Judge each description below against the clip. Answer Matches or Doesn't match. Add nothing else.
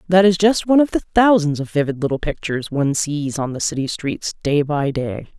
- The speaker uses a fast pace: Matches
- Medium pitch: Matches